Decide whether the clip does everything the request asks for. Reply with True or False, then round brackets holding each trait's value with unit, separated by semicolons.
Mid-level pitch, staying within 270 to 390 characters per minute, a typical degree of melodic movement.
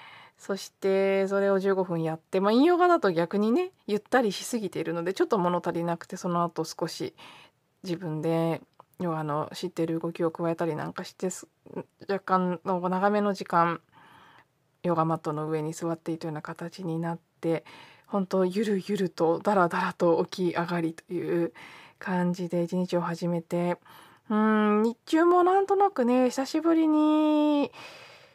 True (180 Hz; 295 characters per minute; 3.5 semitones)